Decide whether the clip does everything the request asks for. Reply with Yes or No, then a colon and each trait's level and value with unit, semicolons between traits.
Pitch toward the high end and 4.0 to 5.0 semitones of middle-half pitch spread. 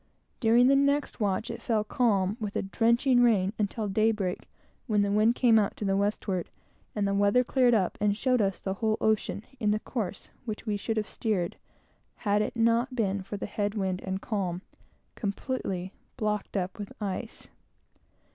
No: high, 210 Hz; narrow, 2.6 semitones